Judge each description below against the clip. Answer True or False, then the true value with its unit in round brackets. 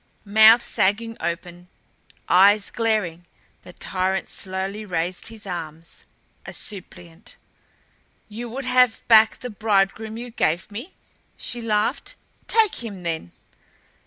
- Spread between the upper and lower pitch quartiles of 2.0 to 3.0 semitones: False (4.1 semitones)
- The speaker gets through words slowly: True (115 wpm)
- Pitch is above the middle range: True (205 Hz)